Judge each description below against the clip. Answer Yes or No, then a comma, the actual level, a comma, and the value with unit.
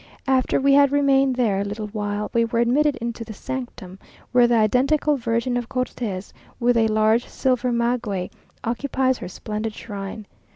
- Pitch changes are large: No, average, 3.2 semitones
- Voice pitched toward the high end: Yes, high, 235 Hz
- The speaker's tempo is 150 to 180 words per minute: Yes, average, 165 wpm